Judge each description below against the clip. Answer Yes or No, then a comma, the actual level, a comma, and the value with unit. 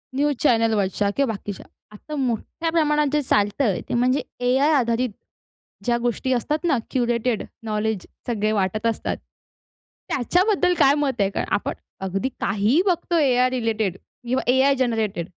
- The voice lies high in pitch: Yes, high, 245 Hz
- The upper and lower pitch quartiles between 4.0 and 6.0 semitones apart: Yes, average, 4.5 semitones